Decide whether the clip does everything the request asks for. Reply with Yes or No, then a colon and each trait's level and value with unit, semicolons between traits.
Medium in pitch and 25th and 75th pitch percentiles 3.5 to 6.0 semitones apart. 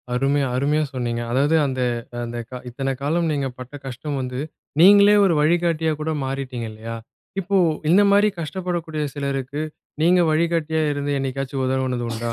Yes: medium, 145 Hz; average, 3.9 semitones